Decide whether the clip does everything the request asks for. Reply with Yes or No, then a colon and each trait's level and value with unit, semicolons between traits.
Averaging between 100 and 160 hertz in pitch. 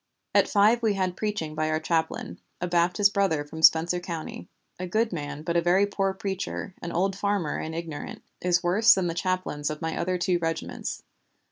No: medium, 175 Hz